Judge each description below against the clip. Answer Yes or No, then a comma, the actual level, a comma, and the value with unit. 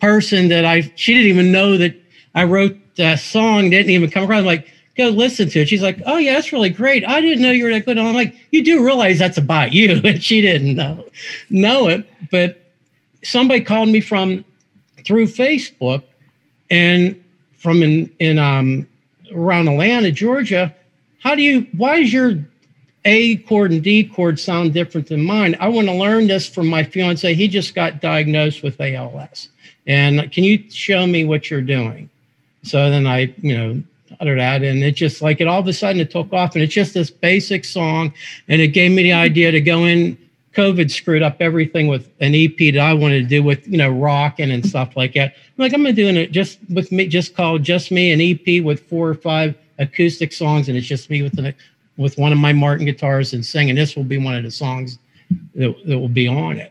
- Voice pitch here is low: No, medium, 170 Hz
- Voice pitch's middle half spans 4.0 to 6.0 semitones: Yes, average, 5.1 semitones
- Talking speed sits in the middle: No, fast, 215 wpm